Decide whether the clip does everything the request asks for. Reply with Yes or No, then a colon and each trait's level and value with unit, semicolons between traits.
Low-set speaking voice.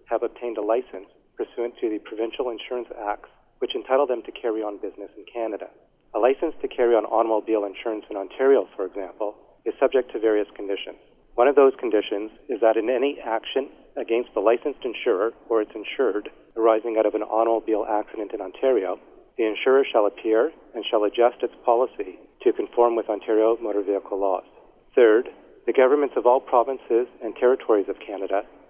Yes: low, 115 Hz